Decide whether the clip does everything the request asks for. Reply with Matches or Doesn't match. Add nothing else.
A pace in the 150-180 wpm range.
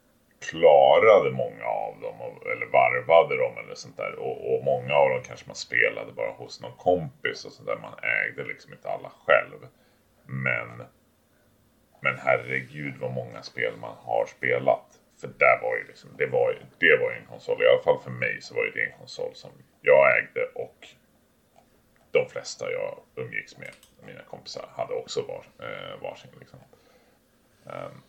Matches